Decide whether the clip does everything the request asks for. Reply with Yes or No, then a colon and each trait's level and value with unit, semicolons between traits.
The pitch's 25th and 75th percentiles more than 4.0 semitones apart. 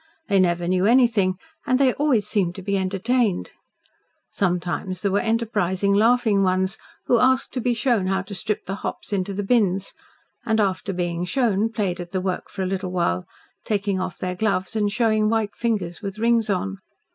No: average, 3.3 semitones